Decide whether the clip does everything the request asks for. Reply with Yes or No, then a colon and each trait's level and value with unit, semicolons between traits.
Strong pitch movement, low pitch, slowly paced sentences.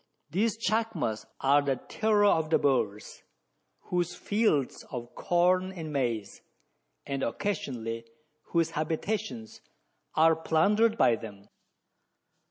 No: wide, 8.2 semitones; medium, 160 Hz; slow, 105 wpm